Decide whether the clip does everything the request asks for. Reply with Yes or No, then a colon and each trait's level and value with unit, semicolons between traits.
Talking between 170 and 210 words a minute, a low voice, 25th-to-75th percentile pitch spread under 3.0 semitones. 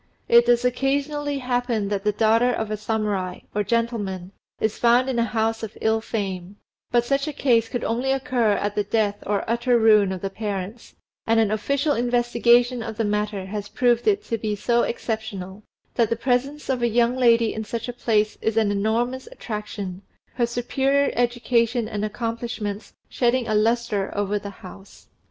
No: average, 180 wpm; high, 230 Hz; narrow, 2.6 semitones